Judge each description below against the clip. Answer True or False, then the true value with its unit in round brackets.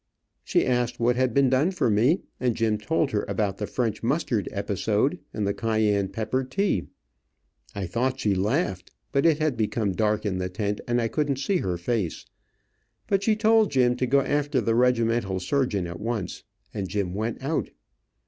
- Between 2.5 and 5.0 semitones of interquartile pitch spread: True (4.7 semitones)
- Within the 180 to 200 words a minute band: True (185 wpm)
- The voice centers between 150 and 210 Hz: False (115 Hz)